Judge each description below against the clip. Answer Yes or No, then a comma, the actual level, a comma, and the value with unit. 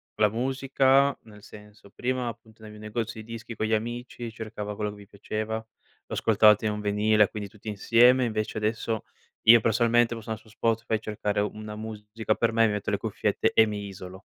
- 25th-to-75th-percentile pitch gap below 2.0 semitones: Yes, narrow, 1.6 semitones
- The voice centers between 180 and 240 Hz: No, low, 110 Hz